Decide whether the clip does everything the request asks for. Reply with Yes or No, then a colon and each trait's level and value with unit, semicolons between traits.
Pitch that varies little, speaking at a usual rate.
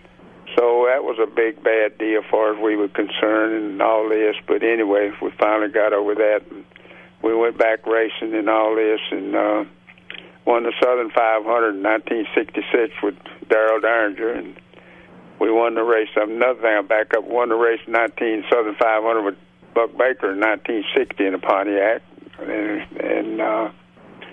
Yes: narrow, 1.2 semitones; average, 170 wpm